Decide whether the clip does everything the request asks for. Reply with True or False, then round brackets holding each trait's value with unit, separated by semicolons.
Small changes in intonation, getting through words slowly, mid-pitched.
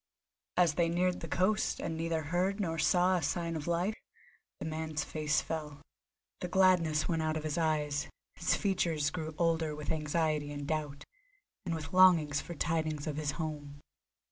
False (2.3 semitones; 170 wpm; 160 Hz)